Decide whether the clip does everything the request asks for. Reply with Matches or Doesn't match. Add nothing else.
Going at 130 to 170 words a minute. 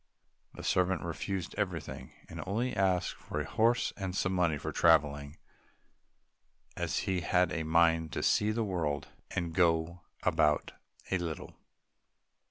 Matches